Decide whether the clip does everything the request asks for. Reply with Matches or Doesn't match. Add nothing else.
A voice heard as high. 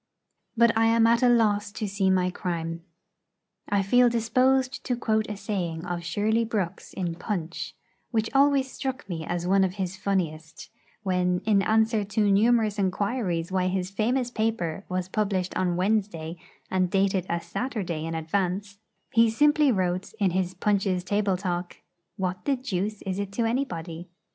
Matches